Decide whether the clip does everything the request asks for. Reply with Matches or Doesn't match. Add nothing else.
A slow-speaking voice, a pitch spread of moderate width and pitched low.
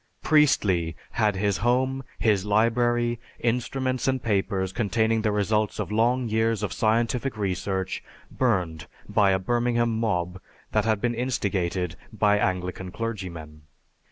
Matches